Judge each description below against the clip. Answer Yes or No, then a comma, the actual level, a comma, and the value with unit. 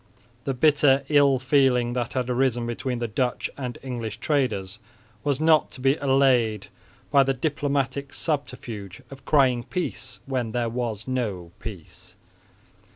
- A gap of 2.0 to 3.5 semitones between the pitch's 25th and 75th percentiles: Yes, average, 2.8 semitones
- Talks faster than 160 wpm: No, average, 140 wpm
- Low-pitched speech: Yes, low, 130 Hz